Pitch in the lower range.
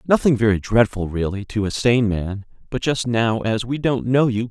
Yes: low, 115 Hz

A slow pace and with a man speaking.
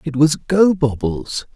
Yes: slow, 115 wpm; male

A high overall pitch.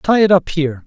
No: medium, 160 Hz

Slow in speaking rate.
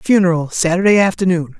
Yes: slow, 115 wpm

